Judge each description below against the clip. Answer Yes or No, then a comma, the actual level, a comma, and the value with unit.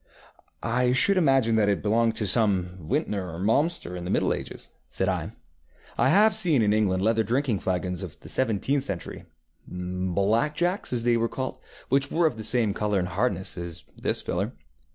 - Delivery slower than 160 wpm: No, average, 175 wpm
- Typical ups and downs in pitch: No, wide, 5.7 semitones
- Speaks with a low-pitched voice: Yes, low, 110 Hz